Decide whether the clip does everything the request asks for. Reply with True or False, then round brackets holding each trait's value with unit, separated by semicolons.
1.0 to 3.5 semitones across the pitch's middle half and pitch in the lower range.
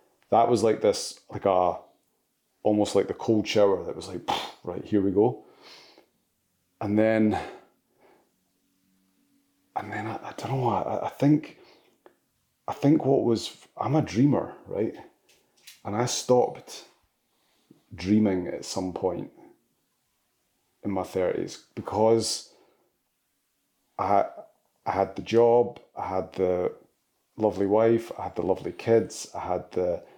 True (3.0 semitones; 105 Hz)